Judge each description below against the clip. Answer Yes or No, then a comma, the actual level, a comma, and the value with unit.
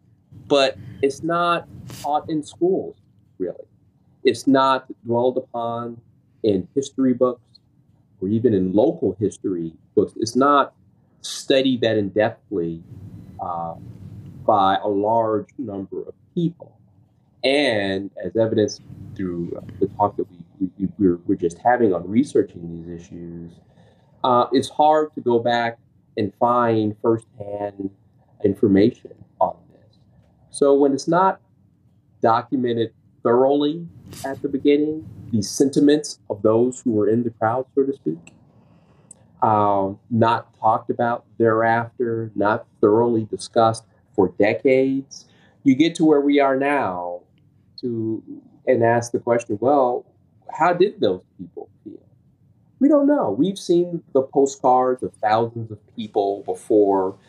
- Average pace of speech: No, slow, 130 wpm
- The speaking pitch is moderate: No, low, 120 Hz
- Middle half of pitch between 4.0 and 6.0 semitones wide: Yes, average, 4.7 semitones